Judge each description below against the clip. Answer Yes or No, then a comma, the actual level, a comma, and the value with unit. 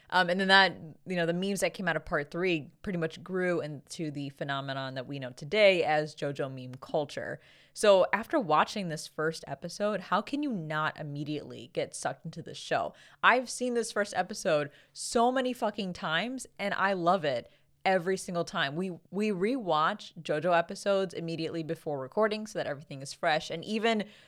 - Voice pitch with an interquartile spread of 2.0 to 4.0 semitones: No, average, 4.5 semitones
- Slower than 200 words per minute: Yes, average, 185 wpm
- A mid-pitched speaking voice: Yes, medium, 170 Hz